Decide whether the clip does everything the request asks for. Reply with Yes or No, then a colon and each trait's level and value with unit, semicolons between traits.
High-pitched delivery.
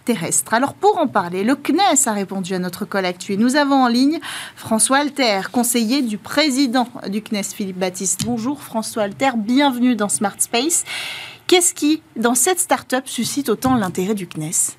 Yes: high, 240 Hz